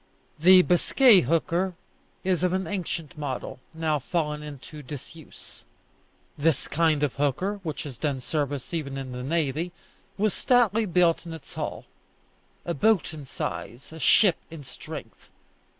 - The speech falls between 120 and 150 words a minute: Yes, average, 145 wpm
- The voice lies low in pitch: No, medium, 160 Hz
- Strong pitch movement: No, average, 4.0 semitones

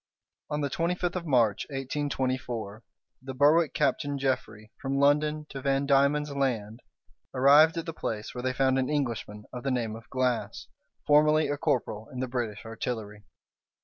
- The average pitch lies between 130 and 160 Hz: Yes, low, 135 Hz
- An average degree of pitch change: Yes, average, 3.8 semitones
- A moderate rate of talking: Yes, average, 165 wpm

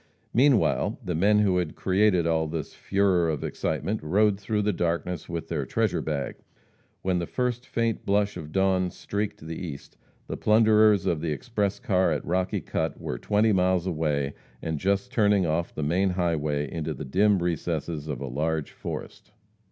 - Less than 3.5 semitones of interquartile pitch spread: No, average, 4.3 semitones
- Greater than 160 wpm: Yes, average, 175 wpm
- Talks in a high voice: No, very low, 90 Hz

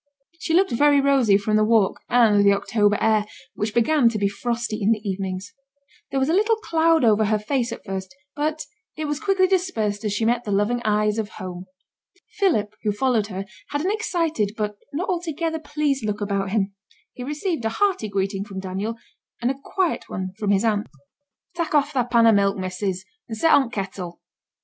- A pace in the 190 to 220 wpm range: Yes, average, 200 wpm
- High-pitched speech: Yes, high, 225 Hz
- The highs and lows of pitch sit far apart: Yes, wide, 6.3 semitones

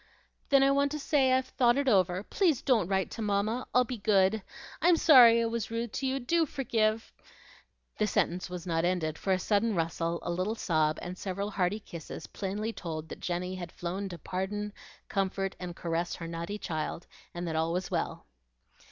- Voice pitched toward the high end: Yes, high, 200 Hz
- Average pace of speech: Yes, average, 195 wpm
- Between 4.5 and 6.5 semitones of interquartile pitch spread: Yes, average, 4.9 semitones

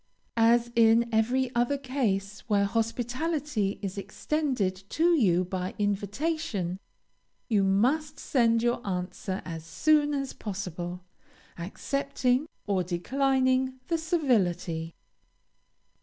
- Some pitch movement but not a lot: No, wide, 6.0 semitones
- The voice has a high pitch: Yes, high, 230 Hz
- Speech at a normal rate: No, slow, 100 wpm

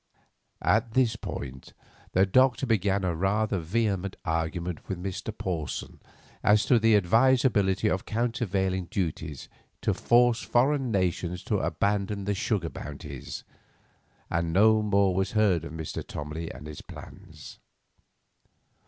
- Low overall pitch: Yes, very low, 95 Hz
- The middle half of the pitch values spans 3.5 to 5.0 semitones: Yes, average, 4.3 semitones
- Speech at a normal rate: No, slow, 125 wpm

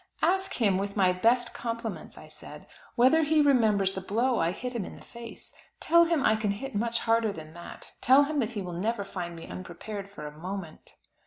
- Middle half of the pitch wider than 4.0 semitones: Yes, average, 4.8 semitones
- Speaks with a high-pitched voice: Yes, high, 215 Hz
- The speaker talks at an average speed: No, fast, 215 wpm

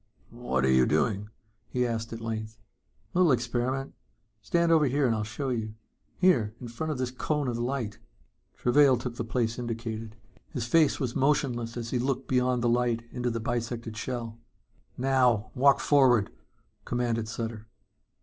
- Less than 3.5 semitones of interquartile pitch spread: Yes, narrow, 2.4 semitones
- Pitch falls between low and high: No, low, 120 Hz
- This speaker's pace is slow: No, average, 160 wpm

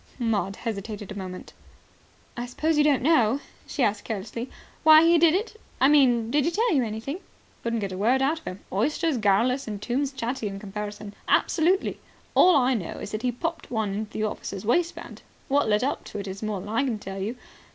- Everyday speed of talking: No, fast, 210 wpm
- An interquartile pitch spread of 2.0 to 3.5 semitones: No, wide, 5.6 semitones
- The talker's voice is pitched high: Yes, high, 235 Hz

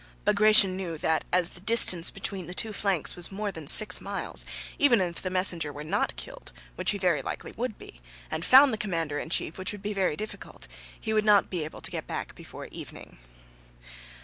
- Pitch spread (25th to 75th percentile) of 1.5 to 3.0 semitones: No, average, 4.1 semitones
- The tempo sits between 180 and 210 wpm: Yes, fast, 205 wpm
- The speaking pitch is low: No, medium, 185 Hz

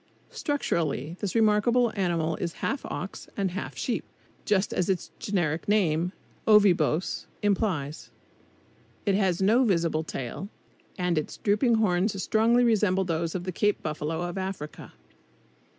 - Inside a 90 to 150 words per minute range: Yes, slow, 135 wpm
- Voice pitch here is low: No, high, 190 Hz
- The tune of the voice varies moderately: Yes, average, 4.0 semitones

